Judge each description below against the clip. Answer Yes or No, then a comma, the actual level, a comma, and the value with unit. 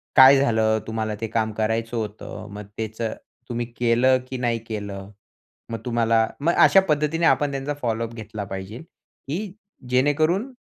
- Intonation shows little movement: No, average, 3.7 semitones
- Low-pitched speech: Yes, low, 115 Hz